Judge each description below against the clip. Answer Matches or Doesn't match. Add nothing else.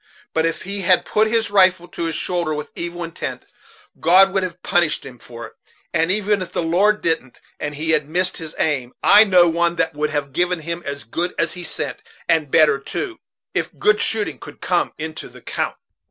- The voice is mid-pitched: Matches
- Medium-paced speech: Doesn't match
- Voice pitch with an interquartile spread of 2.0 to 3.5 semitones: Matches